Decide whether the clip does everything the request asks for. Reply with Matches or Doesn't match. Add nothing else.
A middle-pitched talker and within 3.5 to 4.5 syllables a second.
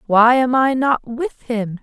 Doesn't match